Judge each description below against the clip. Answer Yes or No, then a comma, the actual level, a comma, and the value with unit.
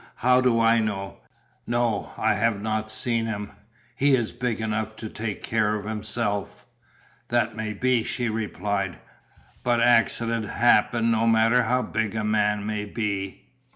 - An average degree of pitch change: No, narrow, 1.8 semitones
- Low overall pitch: Yes, low, 110 Hz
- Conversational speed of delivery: Yes, average, 155 wpm